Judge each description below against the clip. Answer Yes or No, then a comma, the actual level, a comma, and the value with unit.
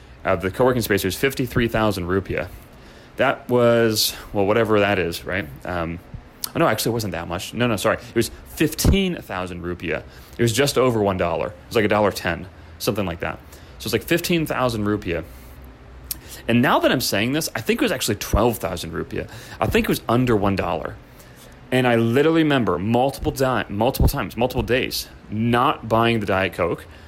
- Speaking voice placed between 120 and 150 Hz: No, low, 110 Hz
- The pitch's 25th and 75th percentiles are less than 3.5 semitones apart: No, wide, 5.6 semitones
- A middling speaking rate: Yes, average, 185 wpm